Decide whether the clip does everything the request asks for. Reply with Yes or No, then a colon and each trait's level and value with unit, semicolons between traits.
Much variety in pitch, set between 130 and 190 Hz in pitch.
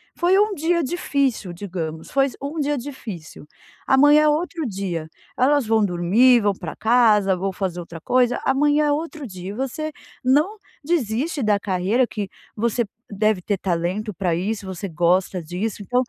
No: wide, 7.1 semitones; high, 220 Hz